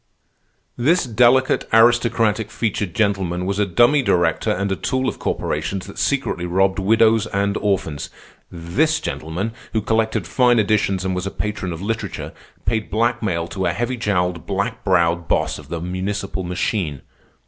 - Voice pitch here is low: Yes, low, 100 Hz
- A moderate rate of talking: Yes, average, 155 wpm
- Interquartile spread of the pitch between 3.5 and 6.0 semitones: Yes, average, 3.9 semitones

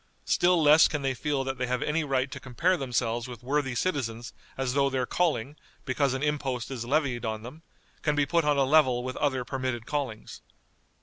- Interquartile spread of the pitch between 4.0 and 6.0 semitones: No, average, 3.0 semitones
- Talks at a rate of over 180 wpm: Yes, average, 200 wpm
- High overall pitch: No, low, 135 Hz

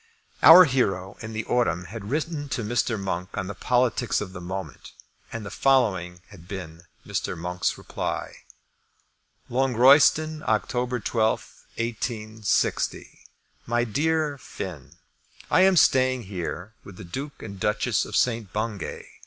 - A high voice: No, low, 110 Hz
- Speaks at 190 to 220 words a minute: No, slow, 135 wpm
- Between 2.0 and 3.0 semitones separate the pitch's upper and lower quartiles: No, average, 5.2 semitones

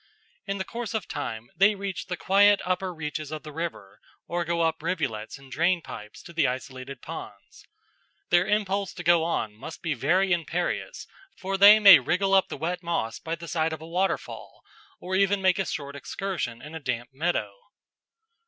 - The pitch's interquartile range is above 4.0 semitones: Yes, average, 4.6 semitones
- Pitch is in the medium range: Yes, medium, 170 Hz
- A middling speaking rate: Yes, average, 185 wpm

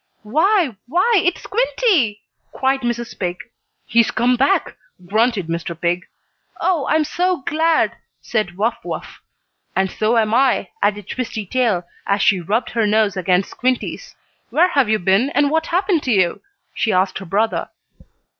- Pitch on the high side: Yes, high, 230 Hz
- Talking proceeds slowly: No, average, 155 wpm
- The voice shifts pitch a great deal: Yes, wide, 7.1 semitones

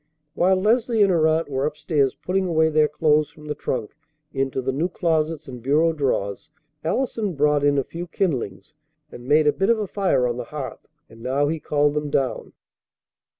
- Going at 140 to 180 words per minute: No, average, 195 wpm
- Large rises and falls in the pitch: No, average, 3.7 semitones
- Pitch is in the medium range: Yes, medium, 150 Hz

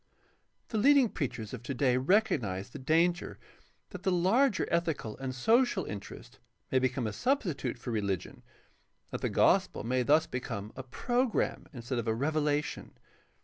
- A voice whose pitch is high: No, medium, 140 Hz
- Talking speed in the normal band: Yes, average, 165 wpm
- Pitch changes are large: Yes, wide, 7.5 semitones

